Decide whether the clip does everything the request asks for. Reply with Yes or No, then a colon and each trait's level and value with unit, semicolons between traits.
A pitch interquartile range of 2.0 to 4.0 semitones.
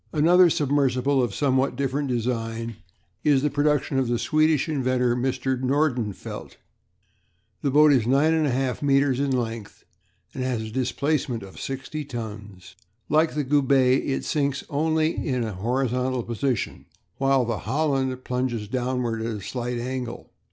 Yes: average, 2.9 semitones